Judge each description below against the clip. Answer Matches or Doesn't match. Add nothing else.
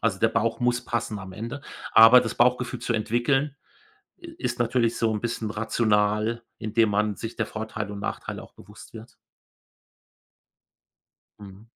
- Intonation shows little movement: Matches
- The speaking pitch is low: Matches